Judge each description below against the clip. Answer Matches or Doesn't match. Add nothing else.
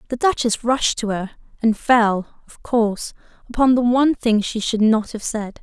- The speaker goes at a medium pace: Matches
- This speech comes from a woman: Matches